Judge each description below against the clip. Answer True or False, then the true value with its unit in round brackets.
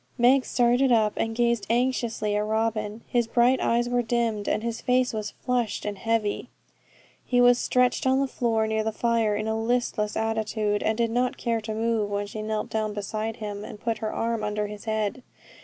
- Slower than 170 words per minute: False (200 wpm)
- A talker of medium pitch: False (225 Hz)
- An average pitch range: False (2.0 semitones)